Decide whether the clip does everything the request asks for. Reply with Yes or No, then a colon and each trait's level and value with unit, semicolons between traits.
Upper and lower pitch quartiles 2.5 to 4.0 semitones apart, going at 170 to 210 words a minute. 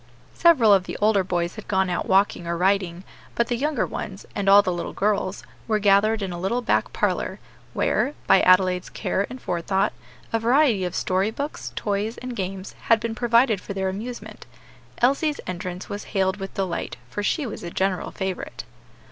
Yes: average, 3.3 semitones; average, 185 wpm